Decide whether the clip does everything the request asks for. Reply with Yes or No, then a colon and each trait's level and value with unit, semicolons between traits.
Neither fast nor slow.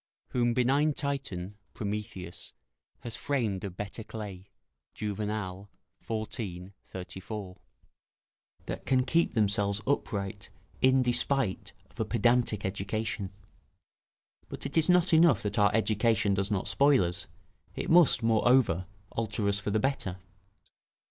No: slow, 120 wpm